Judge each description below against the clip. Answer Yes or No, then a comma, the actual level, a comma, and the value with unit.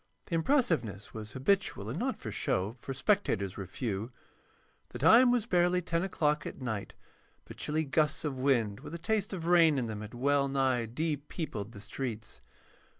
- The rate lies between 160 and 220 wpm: Yes, average, 180 wpm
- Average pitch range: No, wide, 7.4 semitones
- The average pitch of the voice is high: No, medium, 140 Hz